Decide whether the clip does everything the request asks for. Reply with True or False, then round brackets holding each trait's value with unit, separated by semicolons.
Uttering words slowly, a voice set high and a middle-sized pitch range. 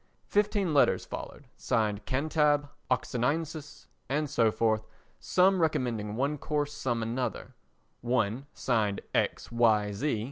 False (105 wpm; 130 Hz; 4.9 semitones)